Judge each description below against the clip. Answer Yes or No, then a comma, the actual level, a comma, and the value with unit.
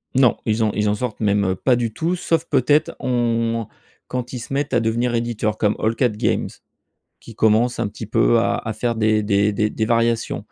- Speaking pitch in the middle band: No, low, 115 Hz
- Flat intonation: Yes, narrow, 2.1 semitones